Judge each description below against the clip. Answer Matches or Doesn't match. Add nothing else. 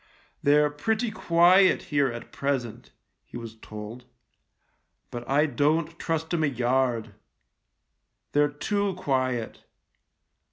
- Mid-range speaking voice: Matches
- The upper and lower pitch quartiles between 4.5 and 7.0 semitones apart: Matches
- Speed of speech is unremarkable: Doesn't match